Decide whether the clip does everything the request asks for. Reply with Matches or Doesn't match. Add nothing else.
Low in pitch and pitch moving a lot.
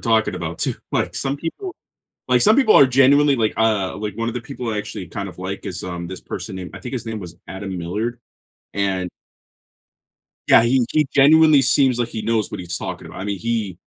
Matches